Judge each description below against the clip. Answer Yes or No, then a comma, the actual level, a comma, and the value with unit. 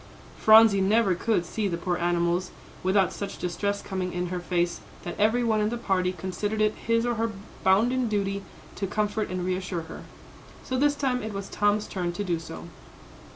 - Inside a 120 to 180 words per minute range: No, average, 190 wpm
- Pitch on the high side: Yes, high, 200 Hz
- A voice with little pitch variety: No, average, 3.3 semitones